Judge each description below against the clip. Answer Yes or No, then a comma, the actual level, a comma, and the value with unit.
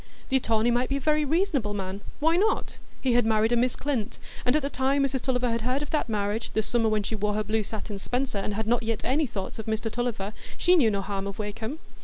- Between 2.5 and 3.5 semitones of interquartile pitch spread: No, average, 3.9 semitones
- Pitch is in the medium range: No, high, 230 Hz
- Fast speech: Yes, fast, 255 wpm